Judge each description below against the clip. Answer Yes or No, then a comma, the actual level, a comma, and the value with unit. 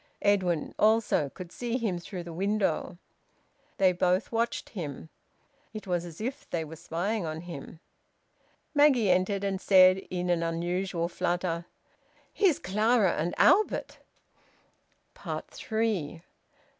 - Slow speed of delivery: Yes, slow, 120 wpm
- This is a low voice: No, medium, 185 Hz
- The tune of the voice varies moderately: Yes, average, 3.8 semitones